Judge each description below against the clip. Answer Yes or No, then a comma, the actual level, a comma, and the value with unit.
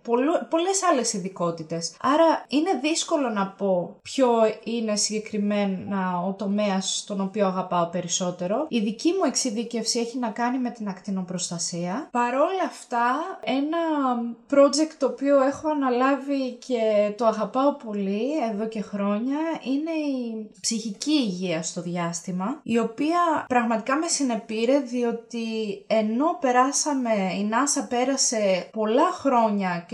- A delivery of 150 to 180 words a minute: No, average, 120 wpm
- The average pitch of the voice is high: Yes, high, 235 Hz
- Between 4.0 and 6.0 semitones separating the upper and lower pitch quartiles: Yes, average, 5.3 semitones